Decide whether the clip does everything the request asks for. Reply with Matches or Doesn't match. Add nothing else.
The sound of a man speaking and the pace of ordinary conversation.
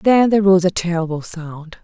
Doesn't match